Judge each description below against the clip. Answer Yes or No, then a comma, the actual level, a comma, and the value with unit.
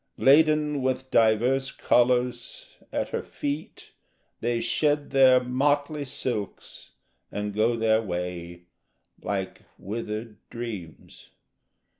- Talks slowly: Yes, slow, 95 wpm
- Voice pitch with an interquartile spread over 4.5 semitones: No, average, 4.0 semitones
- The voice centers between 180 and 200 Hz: No, low, 120 Hz